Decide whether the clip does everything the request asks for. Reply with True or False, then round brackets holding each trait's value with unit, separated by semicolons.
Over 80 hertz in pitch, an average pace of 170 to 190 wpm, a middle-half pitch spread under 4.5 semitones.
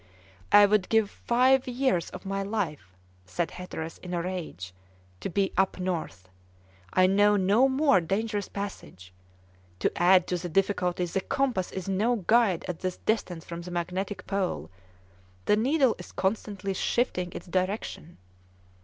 False (190 Hz; 150 wpm; 3.0 semitones)